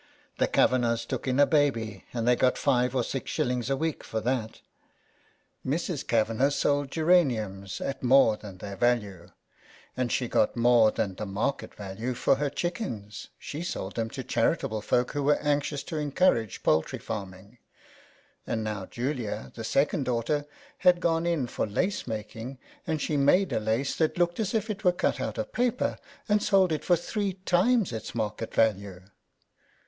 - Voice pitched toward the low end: Yes, low, 125 Hz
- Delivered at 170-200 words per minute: Yes, average, 175 wpm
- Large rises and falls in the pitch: Yes, wide, 5.9 semitones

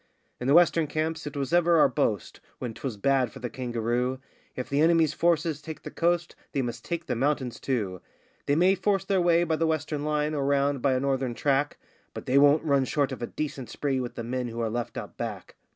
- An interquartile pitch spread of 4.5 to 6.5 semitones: No, average, 4.1 semitones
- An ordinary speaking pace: No, fast, 230 wpm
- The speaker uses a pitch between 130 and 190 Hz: Yes, medium, 140 Hz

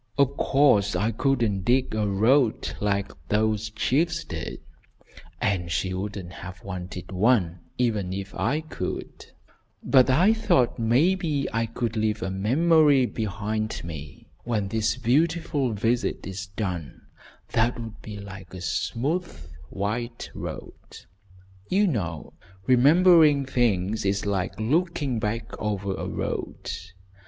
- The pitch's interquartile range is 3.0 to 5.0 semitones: No, wide, 5.4 semitones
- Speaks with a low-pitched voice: Yes, low, 110 Hz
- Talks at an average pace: No, slow, 125 wpm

